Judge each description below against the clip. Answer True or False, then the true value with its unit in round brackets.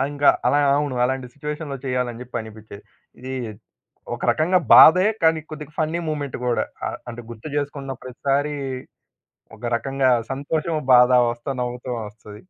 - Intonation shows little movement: False (3.4 semitones)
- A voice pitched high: False (135 Hz)